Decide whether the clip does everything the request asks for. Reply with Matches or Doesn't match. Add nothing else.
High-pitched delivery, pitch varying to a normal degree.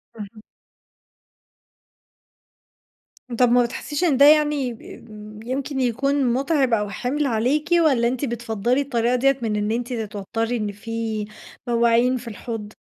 Matches